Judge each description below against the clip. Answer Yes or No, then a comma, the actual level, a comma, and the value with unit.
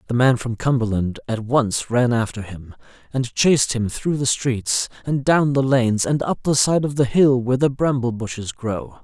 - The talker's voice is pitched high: No, low, 125 Hz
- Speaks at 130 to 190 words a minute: No, fast, 205 wpm